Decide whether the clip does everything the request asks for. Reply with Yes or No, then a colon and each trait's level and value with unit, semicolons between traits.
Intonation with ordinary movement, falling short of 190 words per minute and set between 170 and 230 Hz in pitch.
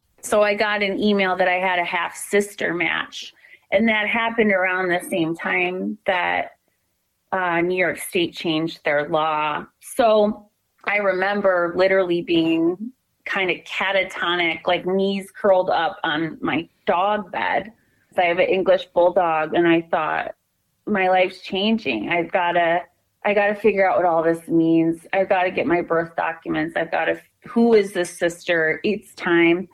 Yes: average, 3.2 semitones; average, 160 wpm; medium, 185 Hz